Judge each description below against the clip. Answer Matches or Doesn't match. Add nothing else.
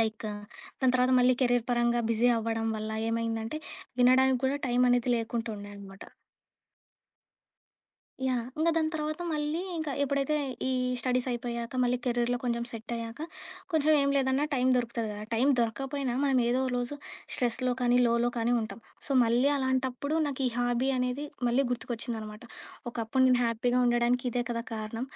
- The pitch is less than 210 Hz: Doesn't match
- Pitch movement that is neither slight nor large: Doesn't match